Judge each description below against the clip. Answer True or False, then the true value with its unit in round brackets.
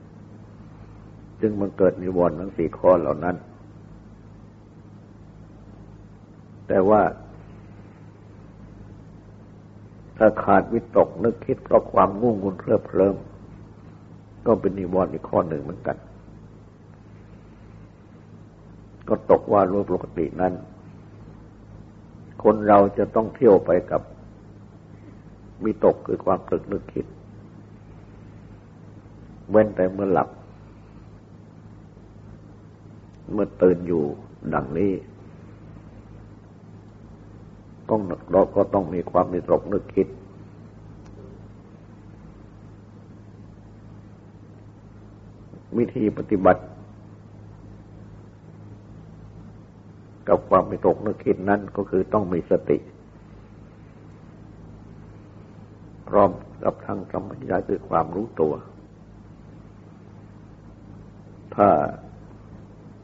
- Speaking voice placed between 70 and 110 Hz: True (100 Hz)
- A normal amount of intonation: False (1.2 semitones)